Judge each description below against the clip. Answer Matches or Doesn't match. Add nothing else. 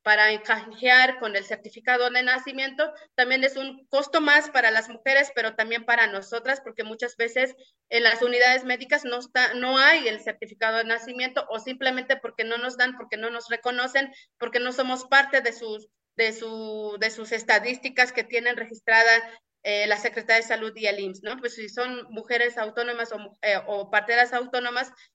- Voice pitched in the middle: Doesn't match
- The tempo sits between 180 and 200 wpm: Matches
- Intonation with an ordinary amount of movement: Doesn't match